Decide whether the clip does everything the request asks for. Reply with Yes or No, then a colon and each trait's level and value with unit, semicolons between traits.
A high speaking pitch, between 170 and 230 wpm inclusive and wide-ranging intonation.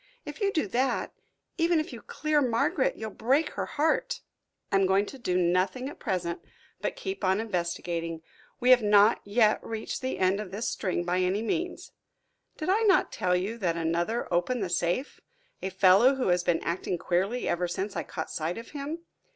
Yes: high, 205 Hz; average, 190 wpm; wide, 6.3 semitones